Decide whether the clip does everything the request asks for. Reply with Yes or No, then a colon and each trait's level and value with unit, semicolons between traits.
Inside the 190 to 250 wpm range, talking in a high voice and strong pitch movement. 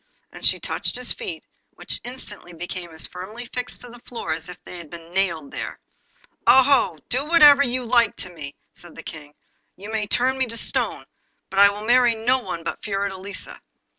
Yes: average, 195 wpm; high, 210 Hz; wide, 6.0 semitones